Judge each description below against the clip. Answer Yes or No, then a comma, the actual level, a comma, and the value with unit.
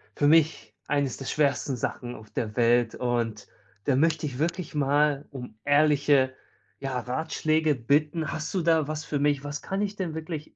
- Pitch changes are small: No, average, 3.1 semitones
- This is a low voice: No, medium, 145 Hz